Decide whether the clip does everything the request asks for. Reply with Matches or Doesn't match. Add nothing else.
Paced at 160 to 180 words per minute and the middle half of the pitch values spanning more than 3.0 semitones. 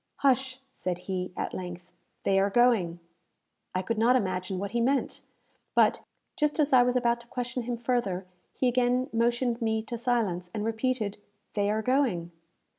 Matches